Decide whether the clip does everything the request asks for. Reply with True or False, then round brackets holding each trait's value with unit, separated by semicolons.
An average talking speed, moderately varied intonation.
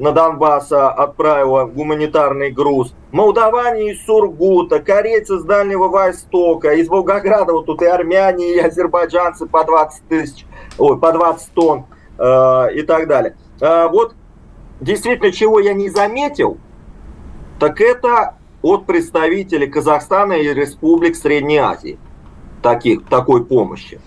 True (125 wpm; 4.8 semitones)